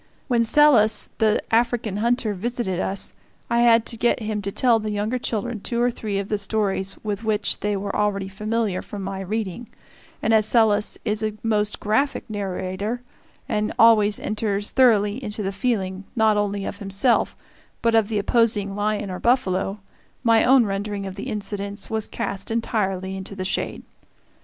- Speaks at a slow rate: No, average, 175 wpm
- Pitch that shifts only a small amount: Yes, narrow, 2.3 semitones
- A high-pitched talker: Yes, high, 210 Hz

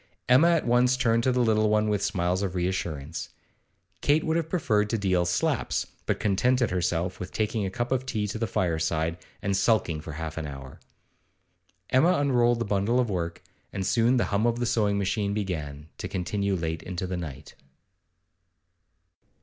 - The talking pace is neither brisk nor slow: Yes, average, 180 wpm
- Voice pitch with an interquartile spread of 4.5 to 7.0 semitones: Yes, average, 5.3 semitones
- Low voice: Yes, low, 100 Hz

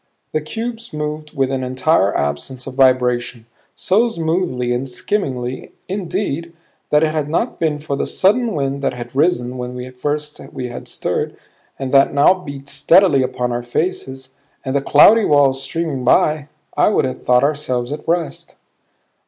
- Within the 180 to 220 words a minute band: No, average, 160 wpm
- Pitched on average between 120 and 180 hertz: Yes, medium, 140 Hz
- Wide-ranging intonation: No, average, 3.9 semitones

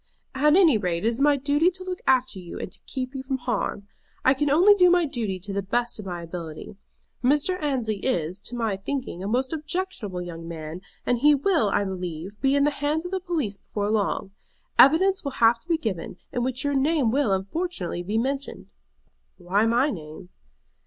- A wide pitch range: Yes, wide, 7.2 semitones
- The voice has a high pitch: Yes, high, 245 Hz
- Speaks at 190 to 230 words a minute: Yes, average, 200 wpm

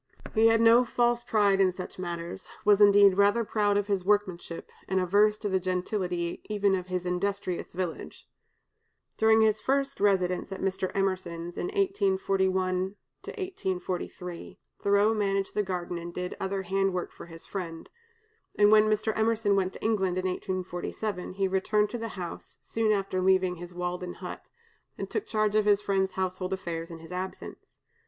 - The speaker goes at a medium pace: Yes, average, 165 wpm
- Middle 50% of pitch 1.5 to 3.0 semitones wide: Yes, narrow, 2.4 semitones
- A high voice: Yes, high, 195 Hz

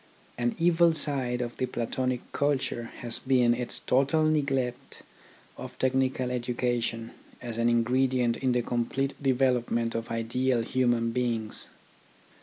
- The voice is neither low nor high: No, low, 125 Hz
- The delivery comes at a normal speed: No, slow, 125 wpm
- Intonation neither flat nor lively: No, narrow, 1.8 semitones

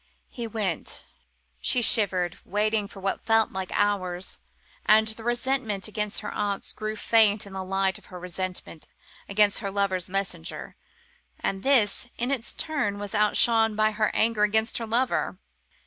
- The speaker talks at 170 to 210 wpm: No, average, 155 wpm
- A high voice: Yes, high, 210 Hz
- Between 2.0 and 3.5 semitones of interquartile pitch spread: Yes, narrow, 2.4 semitones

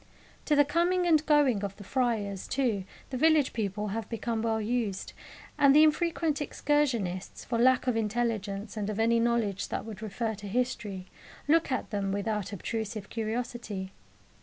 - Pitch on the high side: Yes, high, 230 Hz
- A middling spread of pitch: Yes, average, 4.1 semitones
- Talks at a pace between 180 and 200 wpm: No, average, 160 wpm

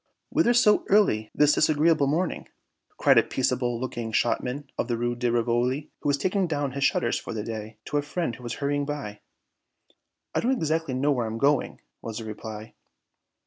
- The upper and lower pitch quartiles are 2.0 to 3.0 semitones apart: No, average, 4.1 semitones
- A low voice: Yes, low, 130 Hz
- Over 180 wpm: Yes, average, 190 wpm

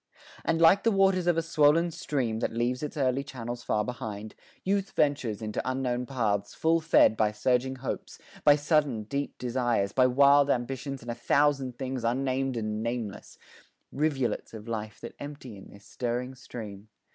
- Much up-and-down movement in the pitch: No, average, 3.8 semitones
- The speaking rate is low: No, average, 170 wpm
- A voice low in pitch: Yes, low, 130 Hz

